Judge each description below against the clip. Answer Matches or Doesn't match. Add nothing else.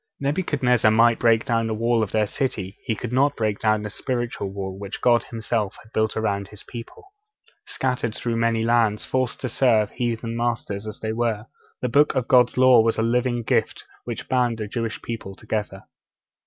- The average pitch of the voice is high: Doesn't match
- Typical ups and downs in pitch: Doesn't match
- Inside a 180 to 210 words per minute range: Matches